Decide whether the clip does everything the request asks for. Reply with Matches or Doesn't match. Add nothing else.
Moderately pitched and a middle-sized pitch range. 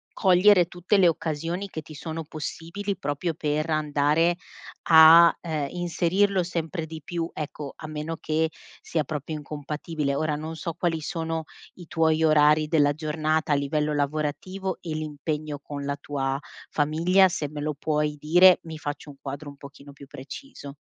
Doesn't match